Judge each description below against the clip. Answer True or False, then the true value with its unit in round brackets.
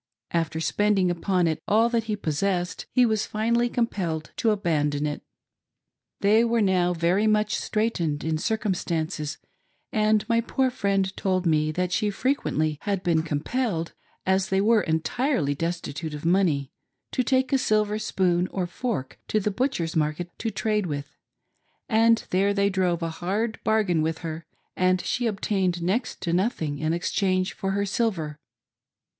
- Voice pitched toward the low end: False (190 Hz)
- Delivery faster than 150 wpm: True (160 wpm)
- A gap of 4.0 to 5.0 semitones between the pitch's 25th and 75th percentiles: True (4.7 semitones)